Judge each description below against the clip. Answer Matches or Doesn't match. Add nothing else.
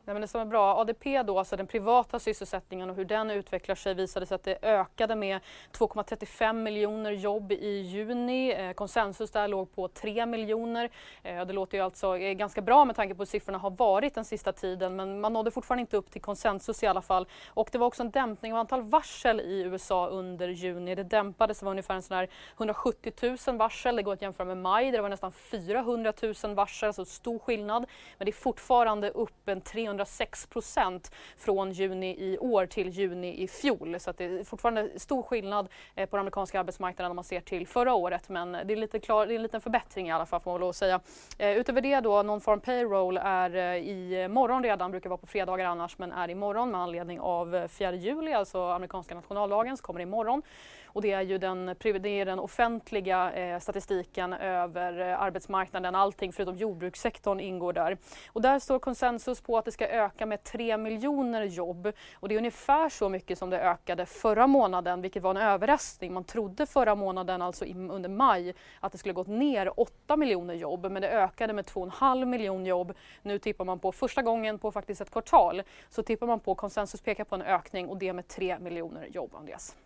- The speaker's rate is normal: Doesn't match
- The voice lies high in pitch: Matches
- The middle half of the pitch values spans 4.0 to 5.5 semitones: Doesn't match